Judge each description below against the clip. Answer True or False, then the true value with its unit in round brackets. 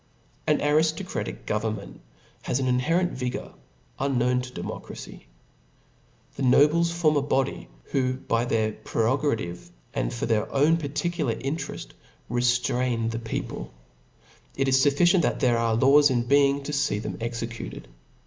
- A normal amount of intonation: True (4.0 semitones)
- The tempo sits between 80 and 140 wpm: True (135 wpm)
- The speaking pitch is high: False (130 Hz)